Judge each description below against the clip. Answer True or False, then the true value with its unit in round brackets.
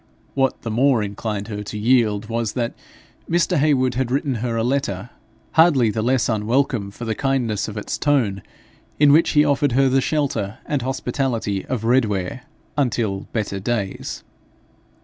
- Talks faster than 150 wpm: True (160 wpm)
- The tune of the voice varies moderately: True (4.1 semitones)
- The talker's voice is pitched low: True (120 Hz)